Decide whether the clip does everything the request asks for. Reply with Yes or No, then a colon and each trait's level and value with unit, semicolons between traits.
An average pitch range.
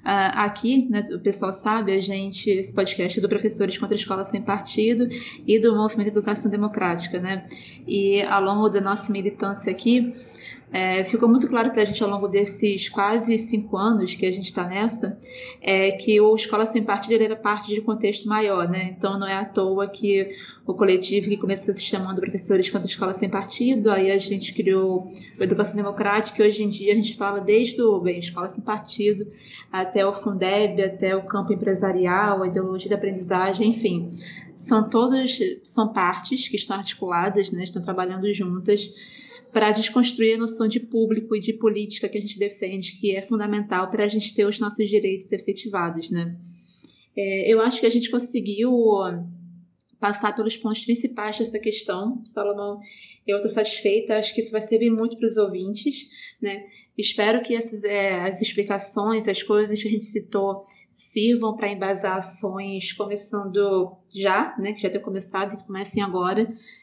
No: narrow, 2.0 semitones